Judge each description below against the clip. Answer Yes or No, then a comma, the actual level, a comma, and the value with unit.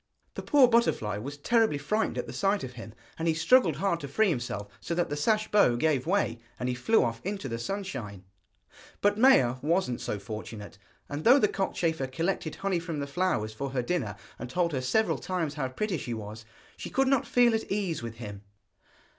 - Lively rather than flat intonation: Yes, wide, 8.4 semitones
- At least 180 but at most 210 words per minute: Yes, fast, 205 wpm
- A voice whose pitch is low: No, medium, 155 Hz